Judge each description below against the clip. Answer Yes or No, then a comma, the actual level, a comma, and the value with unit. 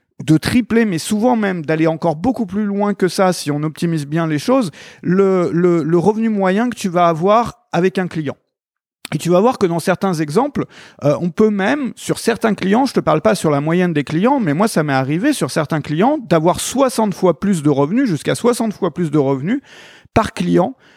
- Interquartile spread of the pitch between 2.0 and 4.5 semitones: No, average, 5.3 semitones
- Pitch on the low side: No, medium, 185 Hz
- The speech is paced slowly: No, fast, 220 wpm